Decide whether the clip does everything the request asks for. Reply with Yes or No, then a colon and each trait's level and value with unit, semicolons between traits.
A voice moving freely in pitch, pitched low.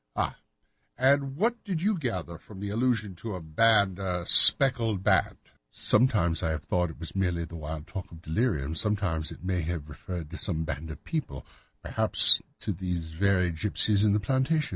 Yes: wide, 5.7 semitones; very low, 95 Hz